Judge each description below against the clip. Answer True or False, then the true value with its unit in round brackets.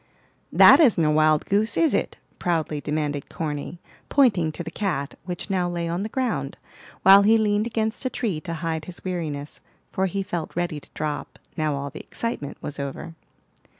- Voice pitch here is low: False (170 Hz)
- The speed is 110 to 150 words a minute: False (185 wpm)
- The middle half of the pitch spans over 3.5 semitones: True (4.8 semitones)